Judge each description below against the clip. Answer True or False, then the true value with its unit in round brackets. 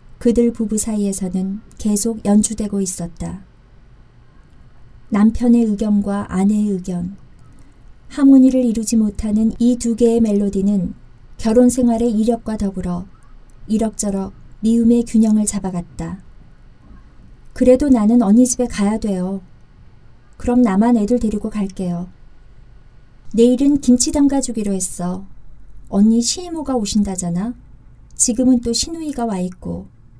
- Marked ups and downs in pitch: False (3.9 semitones)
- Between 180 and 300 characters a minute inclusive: True (260 characters per minute)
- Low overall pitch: False (215 Hz)